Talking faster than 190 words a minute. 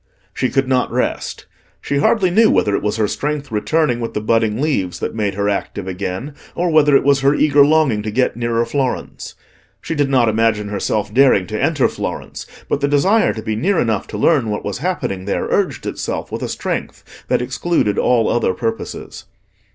Yes: average, 200 wpm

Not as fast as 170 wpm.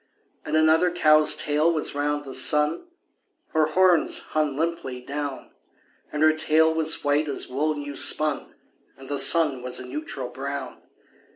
Yes: average, 155 wpm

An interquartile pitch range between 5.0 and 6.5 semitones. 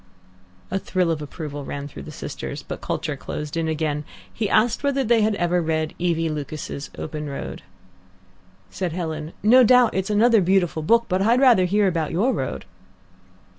Yes: wide, 5.5 semitones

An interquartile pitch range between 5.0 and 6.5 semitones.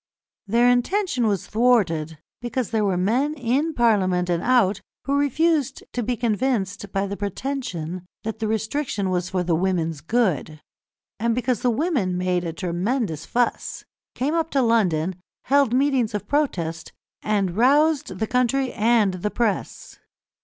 Yes: wide, 5.6 semitones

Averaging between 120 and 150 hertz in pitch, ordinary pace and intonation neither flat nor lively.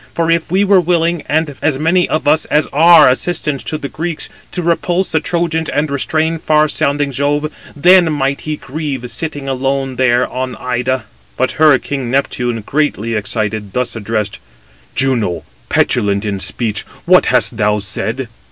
Yes: medium, 140 Hz; average, 160 wpm; average, 4.5 semitones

